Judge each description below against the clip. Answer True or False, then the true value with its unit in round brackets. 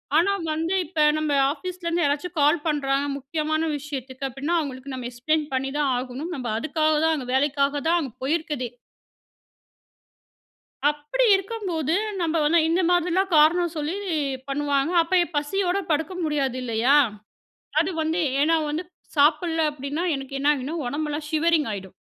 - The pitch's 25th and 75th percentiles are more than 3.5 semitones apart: False (3.2 semitones)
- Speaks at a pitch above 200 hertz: True (300 Hz)